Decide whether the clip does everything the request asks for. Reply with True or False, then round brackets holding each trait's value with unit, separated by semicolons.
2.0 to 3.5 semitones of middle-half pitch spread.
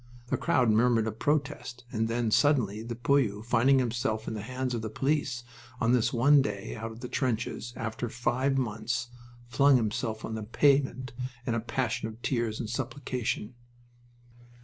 True (2.7 semitones)